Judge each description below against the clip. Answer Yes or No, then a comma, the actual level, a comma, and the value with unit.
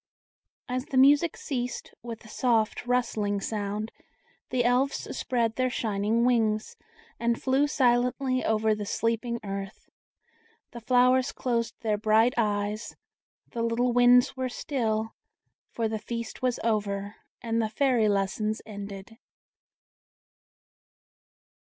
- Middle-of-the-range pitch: No, high, 230 Hz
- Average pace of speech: No, slow, 120 wpm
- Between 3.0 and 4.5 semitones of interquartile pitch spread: No, narrow, 2.6 semitones